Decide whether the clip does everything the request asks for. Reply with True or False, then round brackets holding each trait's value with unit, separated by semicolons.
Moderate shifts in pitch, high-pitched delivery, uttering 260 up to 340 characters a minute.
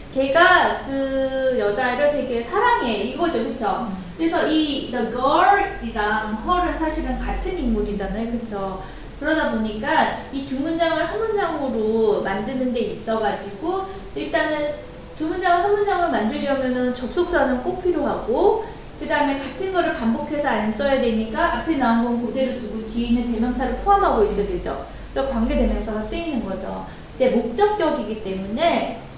False (6.3 semitones; 265 Hz; 335 characters per minute)